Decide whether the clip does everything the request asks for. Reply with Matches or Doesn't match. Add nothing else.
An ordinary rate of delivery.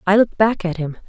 Doesn't match